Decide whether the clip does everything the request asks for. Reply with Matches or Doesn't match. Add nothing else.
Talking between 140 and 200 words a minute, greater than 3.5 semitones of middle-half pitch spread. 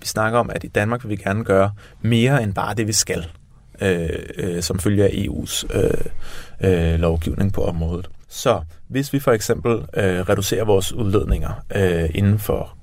Matches